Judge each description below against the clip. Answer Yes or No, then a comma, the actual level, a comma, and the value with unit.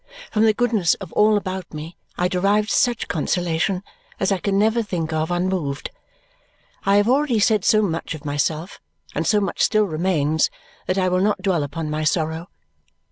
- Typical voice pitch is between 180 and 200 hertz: Yes, medium, 185 Hz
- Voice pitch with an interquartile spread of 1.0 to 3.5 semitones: No, average, 4.4 semitones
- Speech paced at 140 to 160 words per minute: No, average, 180 wpm